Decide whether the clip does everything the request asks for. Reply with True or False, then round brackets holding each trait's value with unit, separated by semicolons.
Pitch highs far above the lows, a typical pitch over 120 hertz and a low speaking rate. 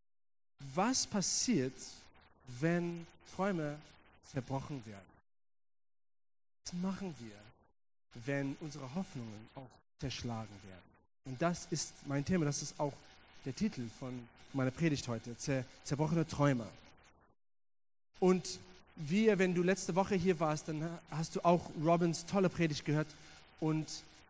True (7.8 semitones; 140 Hz; 120 wpm)